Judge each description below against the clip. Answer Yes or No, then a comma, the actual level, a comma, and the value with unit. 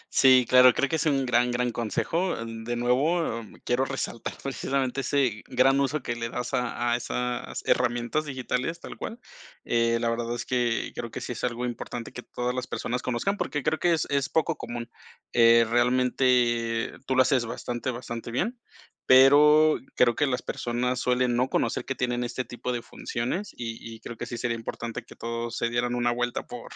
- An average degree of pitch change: No, narrow, 2.1 semitones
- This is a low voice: Yes, low, 125 Hz